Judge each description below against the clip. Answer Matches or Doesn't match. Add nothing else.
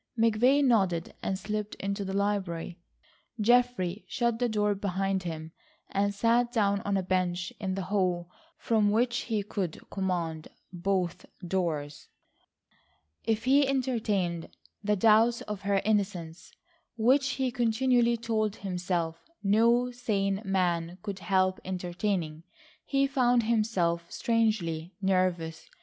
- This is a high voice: Matches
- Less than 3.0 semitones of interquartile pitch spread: Doesn't match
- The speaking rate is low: Matches